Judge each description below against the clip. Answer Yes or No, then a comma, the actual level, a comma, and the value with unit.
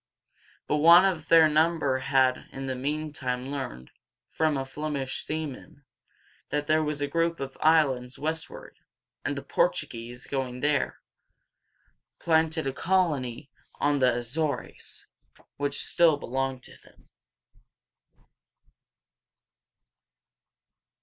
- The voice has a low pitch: No, medium, 145 Hz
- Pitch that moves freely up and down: No, average, 3.3 semitones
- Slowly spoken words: Yes, slow, 110 wpm